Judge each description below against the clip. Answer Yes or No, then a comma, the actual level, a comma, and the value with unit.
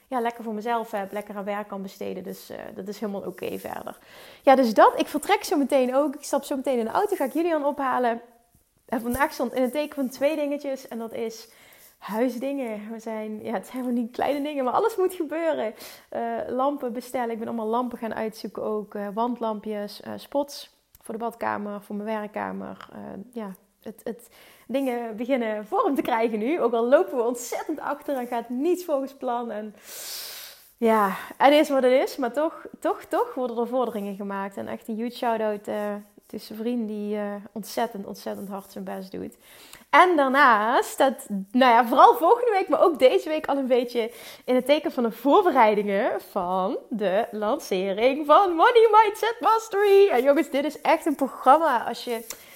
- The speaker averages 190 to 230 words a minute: Yes, fast, 200 wpm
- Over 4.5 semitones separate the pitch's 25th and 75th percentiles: Yes, average, 4.9 semitones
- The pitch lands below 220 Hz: No, high, 245 Hz